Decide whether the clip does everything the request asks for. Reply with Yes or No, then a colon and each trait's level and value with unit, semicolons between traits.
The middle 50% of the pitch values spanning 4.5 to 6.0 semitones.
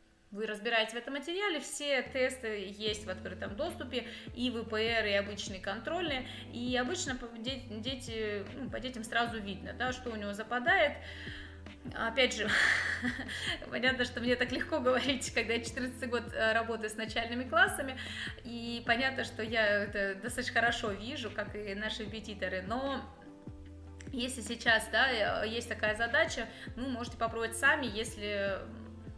No: average, 2.9 semitones